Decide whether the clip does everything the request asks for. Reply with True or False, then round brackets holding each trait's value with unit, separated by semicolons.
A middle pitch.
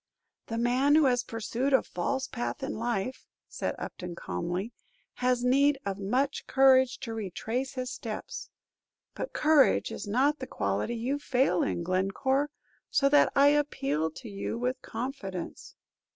False (250 Hz)